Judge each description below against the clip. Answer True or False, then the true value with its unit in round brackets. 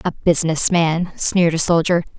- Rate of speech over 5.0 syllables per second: True (5.2 syllables/s)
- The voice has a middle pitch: True (170 Hz)